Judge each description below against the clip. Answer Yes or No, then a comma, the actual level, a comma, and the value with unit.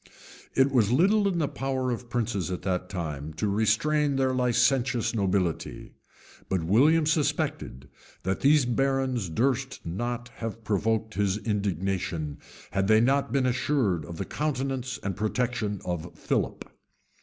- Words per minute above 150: No, average, 145 wpm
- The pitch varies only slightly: No, wide, 5.4 semitones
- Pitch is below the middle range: Yes, low, 115 Hz